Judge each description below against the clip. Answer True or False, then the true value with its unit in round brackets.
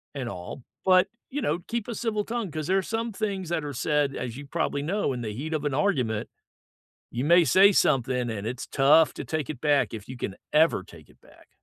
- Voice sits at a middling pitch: True (150 Hz)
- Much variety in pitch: True (6.9 semitones)